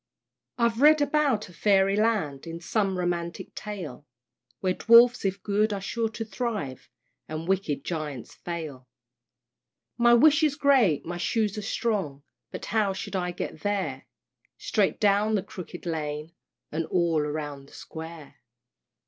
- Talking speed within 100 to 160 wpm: Yes, average, 145 wpm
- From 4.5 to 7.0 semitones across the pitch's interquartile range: Yes, wide, 5.4 semitones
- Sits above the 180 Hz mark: Yes, high, 190 Hz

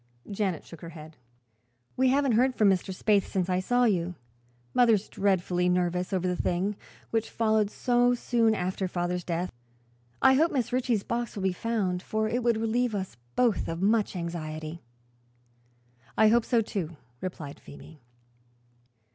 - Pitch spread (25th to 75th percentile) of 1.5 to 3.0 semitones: No, average, 4.4 semitones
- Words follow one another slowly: No, average, 155 wpm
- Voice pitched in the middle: No, high, 200 Hz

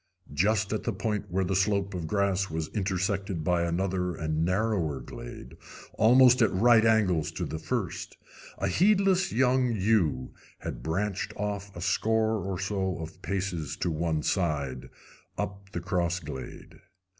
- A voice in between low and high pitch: No, very low, 95 Hz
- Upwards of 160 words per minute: No, average, 150 wpm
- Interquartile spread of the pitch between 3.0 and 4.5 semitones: Yes, average, 3.9 semitones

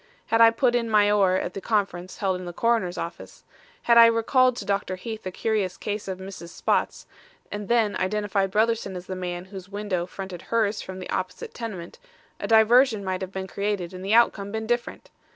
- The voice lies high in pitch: Yes, high, 200 Hz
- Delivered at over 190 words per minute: Yes, fast, 205 wpm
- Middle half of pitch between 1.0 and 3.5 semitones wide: Yes, average, 3.2 semitones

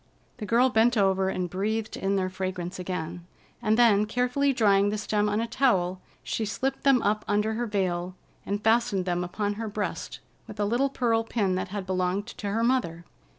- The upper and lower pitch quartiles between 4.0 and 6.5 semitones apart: No, average, 3.4 semitones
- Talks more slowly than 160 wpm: No, average, 195 wpm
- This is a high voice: Yes, high, 205 Hz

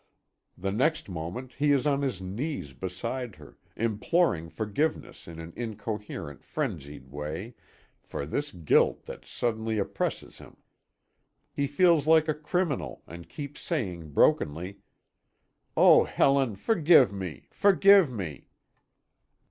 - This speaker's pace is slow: Yes, slow, 120 wpm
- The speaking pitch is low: Yes, low, 110 Hz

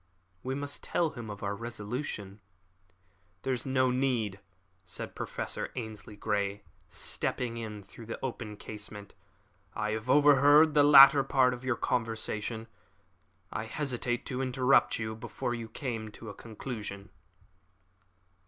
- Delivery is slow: Yes, slow, 130 wpm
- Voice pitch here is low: Yes, low, 115 Hz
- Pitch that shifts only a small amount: No, average, 3.5 semitones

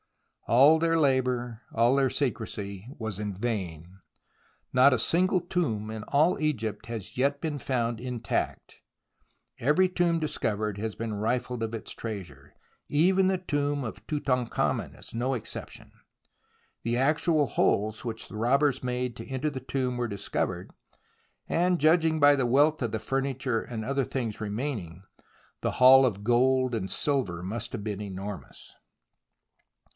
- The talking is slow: No, average, 145 wpm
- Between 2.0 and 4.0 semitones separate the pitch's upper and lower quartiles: No, average, 4.6 semitones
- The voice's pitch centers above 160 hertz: No, low, 125 Hz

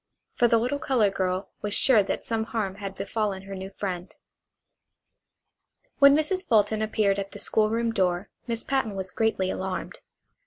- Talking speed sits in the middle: Yes, average, 165 wpm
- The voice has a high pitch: Yes, high, 210 Hz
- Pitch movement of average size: Yes, average, 3.0 semitones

